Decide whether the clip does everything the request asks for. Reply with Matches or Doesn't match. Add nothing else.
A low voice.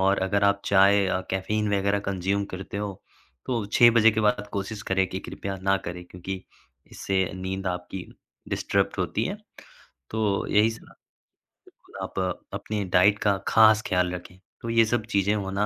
Matches